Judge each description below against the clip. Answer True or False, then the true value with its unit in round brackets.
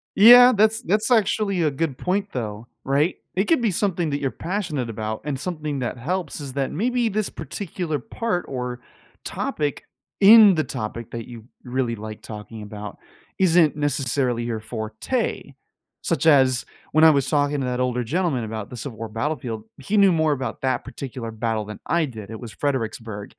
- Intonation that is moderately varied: False (7.2 semitones)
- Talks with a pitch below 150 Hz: True (140 Hz)